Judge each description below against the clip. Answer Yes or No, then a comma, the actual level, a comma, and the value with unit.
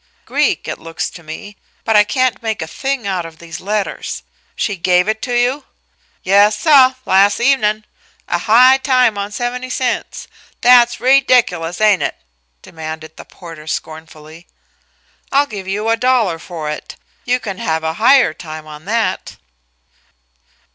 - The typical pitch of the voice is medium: No, high, 210 Hz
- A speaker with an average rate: Yes, average, 155 wpm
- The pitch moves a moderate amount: No, wide, 7.0 semitones